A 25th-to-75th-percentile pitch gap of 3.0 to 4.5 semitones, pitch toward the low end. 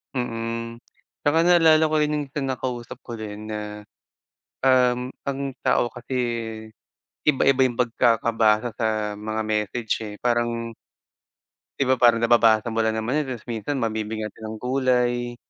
No: narrow, 2.6 semitones; low, 120 Hz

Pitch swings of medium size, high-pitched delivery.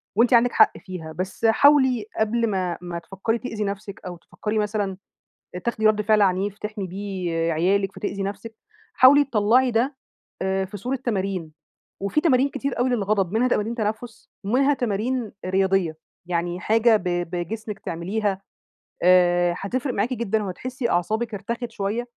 Yes: average, 3.9 semitones; high, 210 Hz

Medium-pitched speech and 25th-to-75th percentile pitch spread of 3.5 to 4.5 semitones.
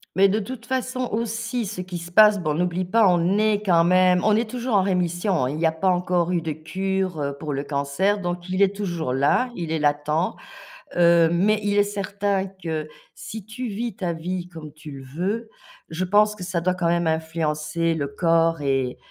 Yes: medium, 180 Hz; average, 4.0 semitones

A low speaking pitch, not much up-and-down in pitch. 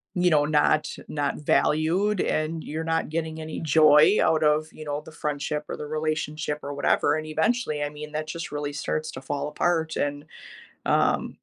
No: medium, 155 Hz; narrow, 1.3 semitones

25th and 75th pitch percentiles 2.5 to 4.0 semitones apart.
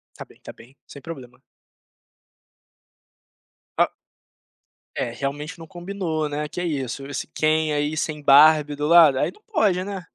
Yes: average, 3.1 semitones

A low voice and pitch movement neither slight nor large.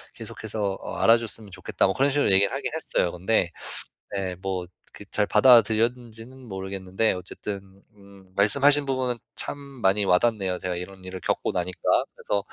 Yes: low, 100 Hz; average, 3.7 semitones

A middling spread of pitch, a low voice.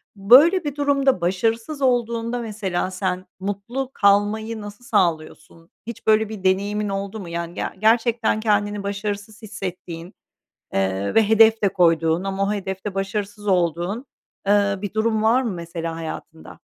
No: average, 3.2 semitones; high, 205 Hz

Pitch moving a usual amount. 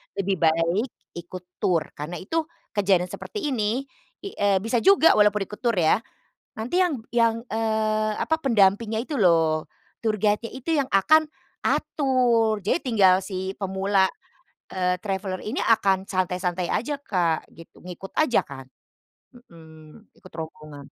Yes: average, 4.3 semitones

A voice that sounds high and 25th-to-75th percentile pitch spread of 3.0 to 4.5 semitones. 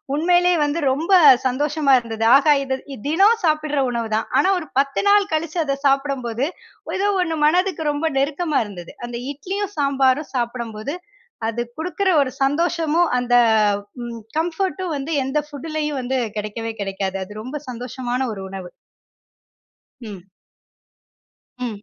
No: very high, 280 Hz; average, 5.0 semitones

